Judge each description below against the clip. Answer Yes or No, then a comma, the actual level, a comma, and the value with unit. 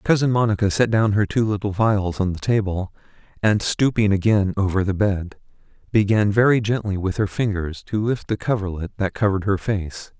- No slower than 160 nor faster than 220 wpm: Yes, average, 180 wpm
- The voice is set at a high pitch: No, low, 100 Hz